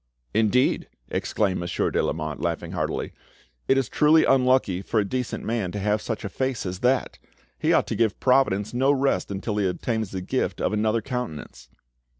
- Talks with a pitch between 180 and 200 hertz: No, low, 110 Hz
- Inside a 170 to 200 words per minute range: Yes, average, 180 wpm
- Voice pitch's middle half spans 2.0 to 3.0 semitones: No, average, 4.8 semitones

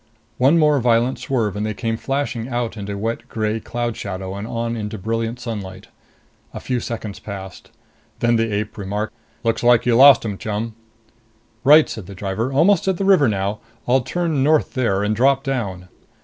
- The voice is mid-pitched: No, low, 115 Hz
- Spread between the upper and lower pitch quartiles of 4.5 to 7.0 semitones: No, average, 3.9 semitones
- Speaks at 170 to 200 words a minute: Yes, average, 180 wpm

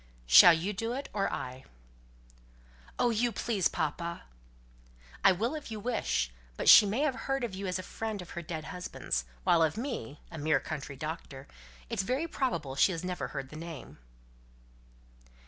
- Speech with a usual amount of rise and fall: No, wide, 6.6 semitones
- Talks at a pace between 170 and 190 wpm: Yes, average, 175 wpm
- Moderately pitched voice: Yes, medium, 180 Hz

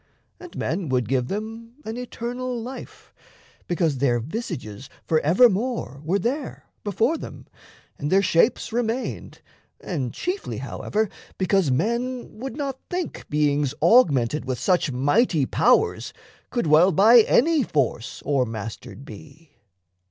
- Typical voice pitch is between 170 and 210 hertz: Yes, high, 190 Hz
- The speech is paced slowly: Yes, slow, 120 wpm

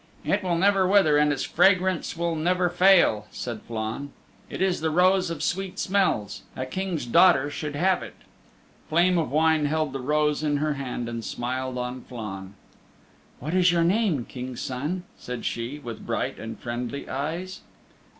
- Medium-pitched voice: Yes, medium, 150 Hz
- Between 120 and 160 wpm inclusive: No, average, 170 wpm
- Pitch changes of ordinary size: No, wide, 6.2 semitones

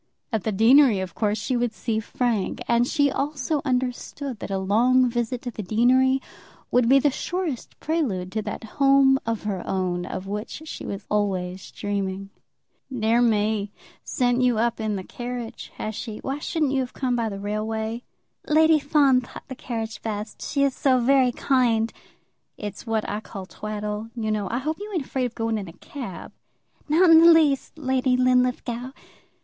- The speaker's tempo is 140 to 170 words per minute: No, average, 180 wpm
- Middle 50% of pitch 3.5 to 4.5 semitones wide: Yes, average, 4.0 semitones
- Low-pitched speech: No, high, 240 Hz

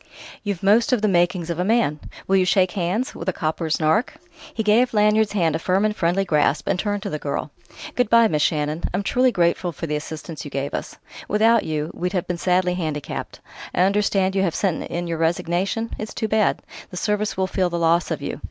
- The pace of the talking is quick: Yes, fast, 225 wpm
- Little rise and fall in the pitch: No, average, 4.1 semitones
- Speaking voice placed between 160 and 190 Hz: Yes, medium, 185 Hz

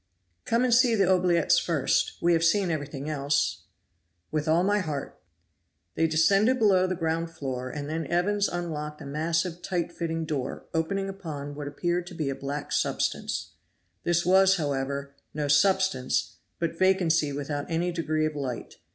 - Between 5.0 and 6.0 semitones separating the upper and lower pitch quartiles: No, average, 3.9 semitones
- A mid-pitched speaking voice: Yes, medium, 165 Hz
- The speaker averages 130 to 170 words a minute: Yes, average, 160 wpm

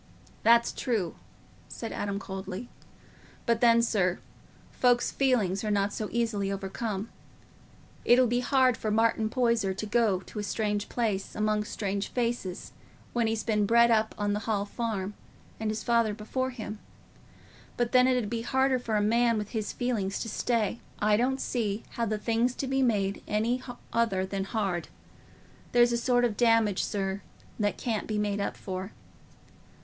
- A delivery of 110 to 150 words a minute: No, average, 165 wpm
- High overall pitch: Yes, high, 220 Hz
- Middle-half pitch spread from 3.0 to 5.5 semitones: No, narrow, 2.6 semitones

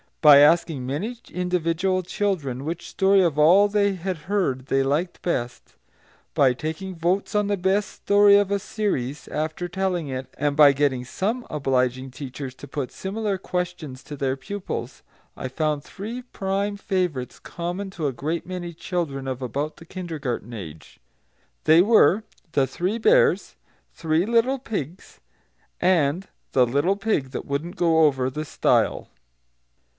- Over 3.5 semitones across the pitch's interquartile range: Yes, wide, 5.6 semitones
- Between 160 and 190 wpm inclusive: No, average, 150 wpm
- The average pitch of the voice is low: No, medium, 165 Hz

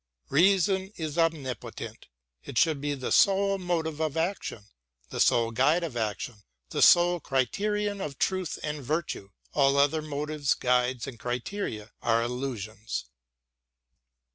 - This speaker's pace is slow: Yes, slow, 130 wpm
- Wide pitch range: Yes, wide, 5.7 semitones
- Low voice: No, medium, 145 Hz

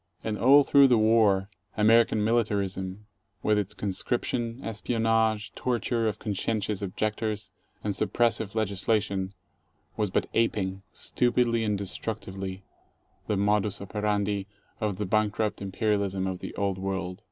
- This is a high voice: No, low, 105 Hz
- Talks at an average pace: No, slow, 125 wpm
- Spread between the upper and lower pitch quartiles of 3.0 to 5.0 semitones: No, narrow, 2.4 semitones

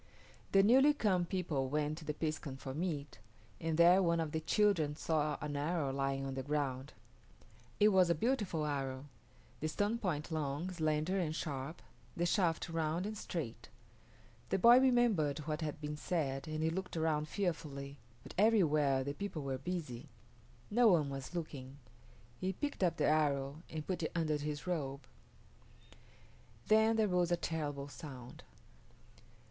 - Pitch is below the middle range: No, medium, 155 Hz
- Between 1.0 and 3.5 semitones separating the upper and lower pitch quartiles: No, average, 4.0 semitones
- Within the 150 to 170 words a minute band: Yes, average, 160 wpm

